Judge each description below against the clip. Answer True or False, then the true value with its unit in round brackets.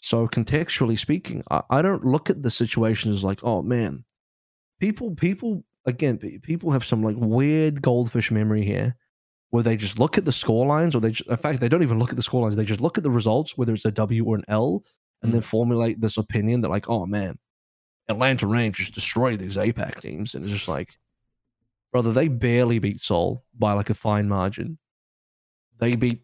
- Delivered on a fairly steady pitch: False (3.1 semitones)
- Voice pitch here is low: True (115 Hz)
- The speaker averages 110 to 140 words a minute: False (205 wpm)